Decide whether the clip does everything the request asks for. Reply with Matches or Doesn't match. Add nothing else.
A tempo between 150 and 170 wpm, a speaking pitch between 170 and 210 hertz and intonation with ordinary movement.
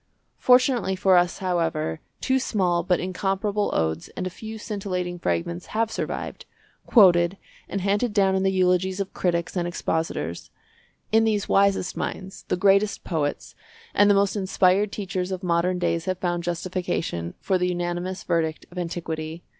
Doesn't match